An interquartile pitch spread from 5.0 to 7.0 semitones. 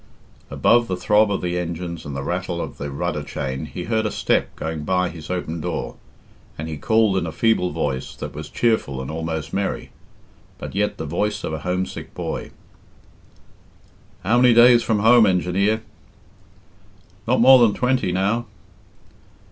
Yes: wide, 5.5 semitones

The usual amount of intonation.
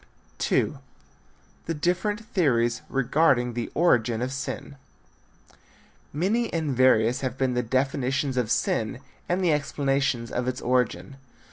Yes: average, 3.3 semitones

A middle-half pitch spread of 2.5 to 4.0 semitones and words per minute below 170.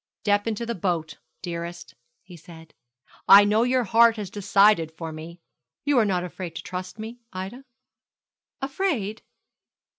No: average, 4.6 semitones; average, 145 wpm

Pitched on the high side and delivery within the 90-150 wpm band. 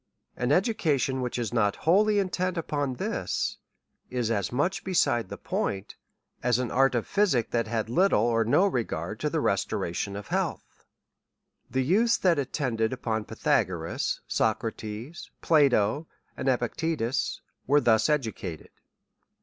No: low, 125 Hz; average, 140 wpm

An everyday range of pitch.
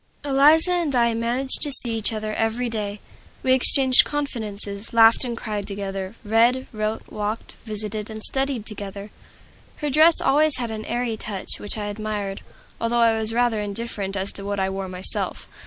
Yes: average, 3.2 semitones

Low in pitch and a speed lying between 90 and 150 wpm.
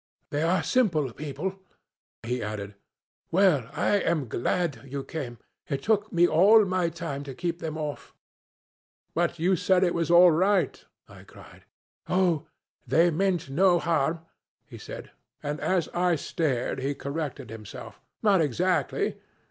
No: medium, 165 Hz; average, 145 wpm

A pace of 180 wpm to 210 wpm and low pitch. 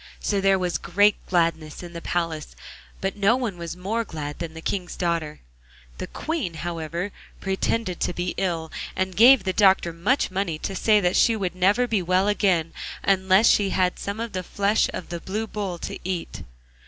No: average, 190 wpm; medium, 185 Hz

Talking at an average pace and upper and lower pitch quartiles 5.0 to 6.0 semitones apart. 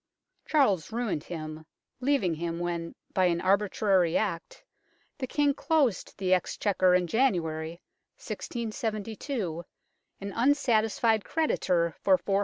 No: slow, 115 wpm; average, 5.3 semitones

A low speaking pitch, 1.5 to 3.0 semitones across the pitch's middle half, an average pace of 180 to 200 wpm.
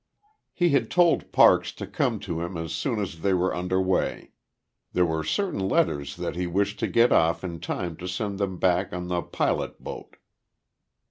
Yes: very low, 90 Hz; average, 2.7 semitones; average, 190 wpm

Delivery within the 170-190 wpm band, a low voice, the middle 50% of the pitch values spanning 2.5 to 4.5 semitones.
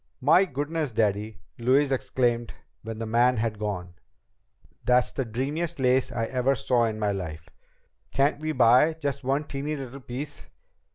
No: average, 155 wpm; low, 125 Hz; average, 3.9 semitones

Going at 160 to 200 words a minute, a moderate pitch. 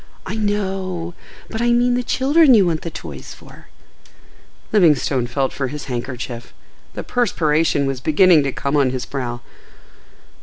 No: average, 145 wpm; medium, 160 Hz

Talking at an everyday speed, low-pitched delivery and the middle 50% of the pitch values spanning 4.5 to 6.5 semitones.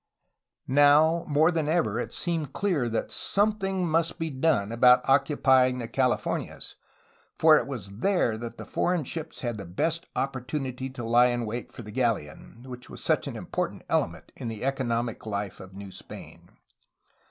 Yes: average, 165 wpm; low, 130 Hz; average, 5.3 semitones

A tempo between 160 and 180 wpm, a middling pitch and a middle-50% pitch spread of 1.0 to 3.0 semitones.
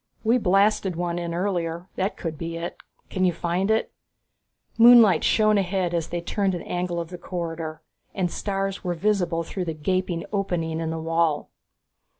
Yes: average, 170 wpm; medium, 175 Hz; average, 2.7 semitones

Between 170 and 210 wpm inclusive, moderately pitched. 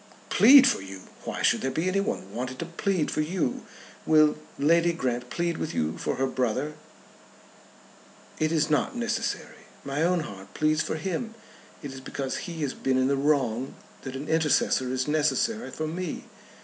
Yes: average, 175 wpm; medium, 150 Hz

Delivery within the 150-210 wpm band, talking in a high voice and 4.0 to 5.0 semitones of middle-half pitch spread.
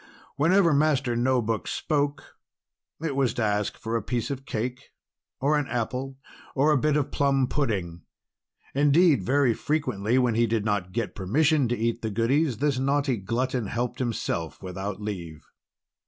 No: average, 160 wpm; low, 125 Hz; average, 4.4 semitones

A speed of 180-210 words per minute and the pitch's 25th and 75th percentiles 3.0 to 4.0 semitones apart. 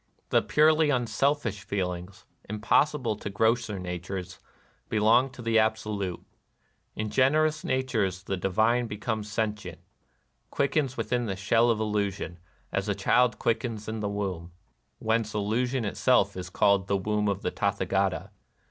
No: average, 145 wpm; average, 3.3 semitones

